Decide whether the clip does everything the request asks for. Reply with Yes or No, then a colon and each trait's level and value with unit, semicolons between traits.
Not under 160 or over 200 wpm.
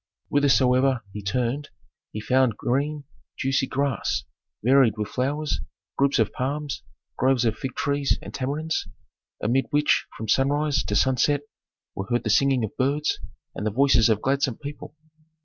No: average, 150 wpm